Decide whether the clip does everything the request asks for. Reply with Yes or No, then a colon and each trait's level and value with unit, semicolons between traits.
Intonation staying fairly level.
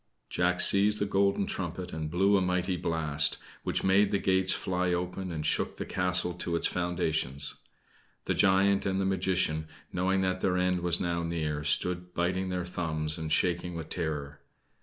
Yes: narrow, 2.3 semitones